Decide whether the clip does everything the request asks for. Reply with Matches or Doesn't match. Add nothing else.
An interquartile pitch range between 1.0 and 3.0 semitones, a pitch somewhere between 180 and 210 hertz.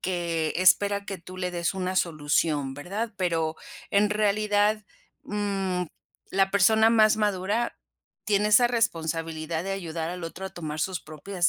Doesn't match